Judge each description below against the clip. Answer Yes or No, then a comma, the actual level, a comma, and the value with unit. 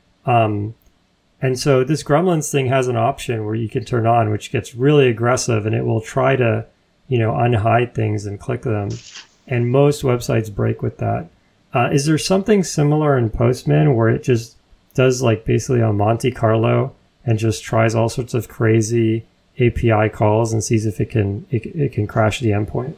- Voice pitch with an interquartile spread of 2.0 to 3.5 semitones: Yes, average, 2.8 semitones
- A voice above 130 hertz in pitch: No, low, 120 Hz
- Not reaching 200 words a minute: Yes, average, 190 wpm